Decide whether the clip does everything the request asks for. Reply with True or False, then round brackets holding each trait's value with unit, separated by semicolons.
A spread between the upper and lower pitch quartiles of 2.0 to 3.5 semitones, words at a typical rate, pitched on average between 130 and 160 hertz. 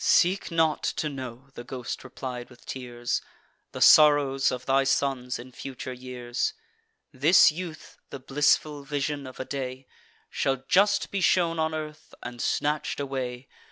True (3.1 semitones; 150 wpm; 135 Hz)